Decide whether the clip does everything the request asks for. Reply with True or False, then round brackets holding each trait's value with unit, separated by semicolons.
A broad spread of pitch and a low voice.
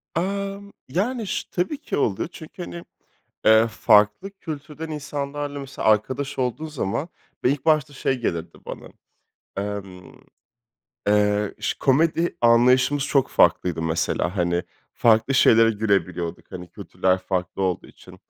True (7.4 semitones; 125 Hz)